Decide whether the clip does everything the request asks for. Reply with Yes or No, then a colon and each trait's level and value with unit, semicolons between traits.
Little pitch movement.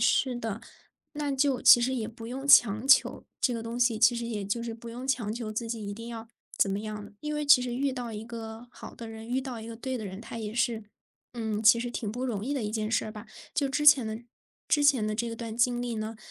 Yes: narrow, 2.2 semitones